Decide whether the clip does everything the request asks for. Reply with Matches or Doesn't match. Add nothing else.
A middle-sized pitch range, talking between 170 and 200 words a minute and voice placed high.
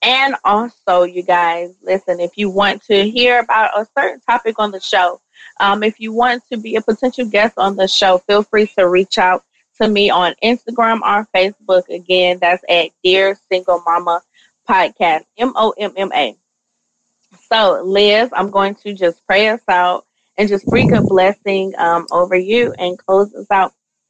Matches